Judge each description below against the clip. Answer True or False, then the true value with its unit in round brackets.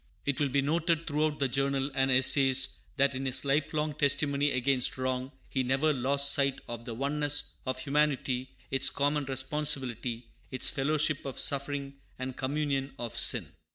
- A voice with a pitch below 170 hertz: True (140 Hz)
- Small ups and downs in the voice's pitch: True (1.8 semitones)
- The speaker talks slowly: False (155 wpm)